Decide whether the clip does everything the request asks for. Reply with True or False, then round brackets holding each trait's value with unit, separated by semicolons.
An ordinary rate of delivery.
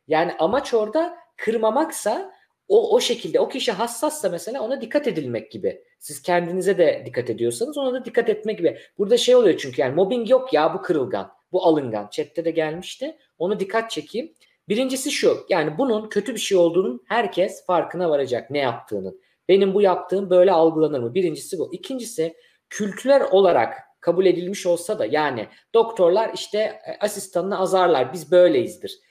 False (160 wpm)